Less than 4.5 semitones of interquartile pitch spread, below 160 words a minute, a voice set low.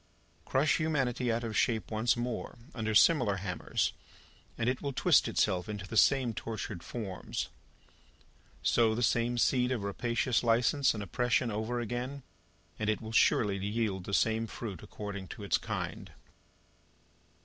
Yes: average, 2.9 semitones; average, 150 wpm; low, 115 Hz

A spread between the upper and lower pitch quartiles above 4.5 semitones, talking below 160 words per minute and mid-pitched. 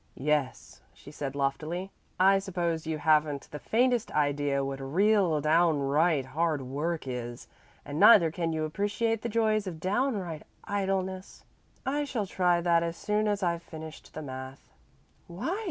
Yes: average, 5.0 semitones; average, 150 wpm; medium, 170 Hz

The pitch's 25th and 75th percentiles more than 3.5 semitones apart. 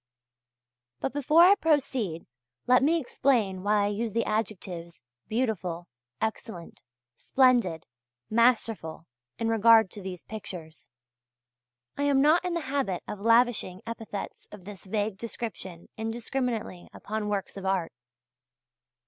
Yes: average, 4.6 semitones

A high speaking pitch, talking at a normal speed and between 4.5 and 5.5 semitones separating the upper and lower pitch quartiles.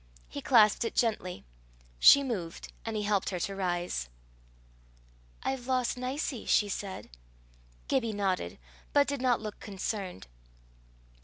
No: high, 210 Hz; slow, 130 wpm; average, 4.9 semitones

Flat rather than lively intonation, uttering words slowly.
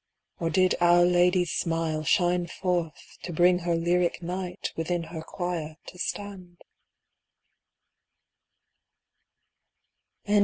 Yes: narrow, 1.3 semitones; slow, 100 wpm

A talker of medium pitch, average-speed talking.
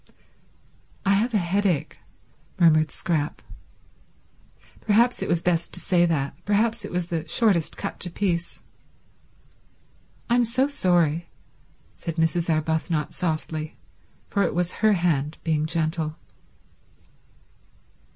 No: medium, 170 Hz; slow, 115 wpm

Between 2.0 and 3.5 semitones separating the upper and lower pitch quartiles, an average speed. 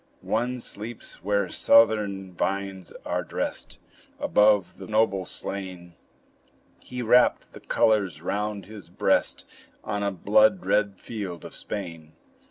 No: narrow, 2.5 semitones; slow, 120 wpm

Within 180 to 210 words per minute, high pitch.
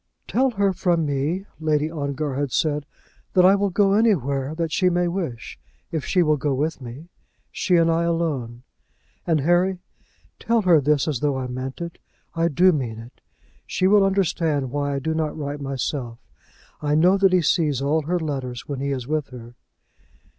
No: average, 185 wpm; medium, 155 Hz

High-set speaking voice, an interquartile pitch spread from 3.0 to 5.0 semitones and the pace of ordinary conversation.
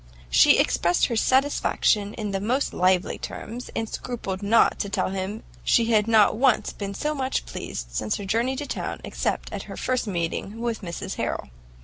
Yes: high, 215 Hz; average, 3.7 semitones; average, 185 wpm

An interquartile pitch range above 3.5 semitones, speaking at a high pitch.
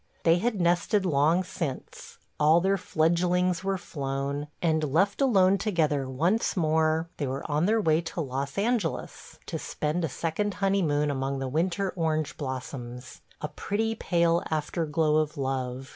No: average, 4.2 semitones; medium, 160 Hz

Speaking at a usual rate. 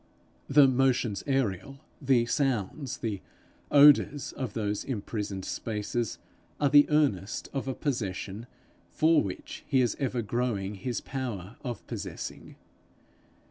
No: slow, 115 wpm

